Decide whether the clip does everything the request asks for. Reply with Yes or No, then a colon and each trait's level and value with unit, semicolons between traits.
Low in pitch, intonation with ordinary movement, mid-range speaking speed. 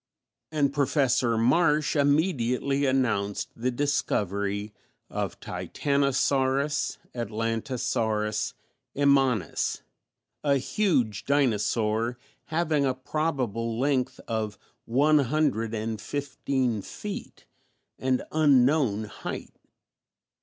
No: low, 130 Hz; average, 4.0 semitones; slow, 80 wpm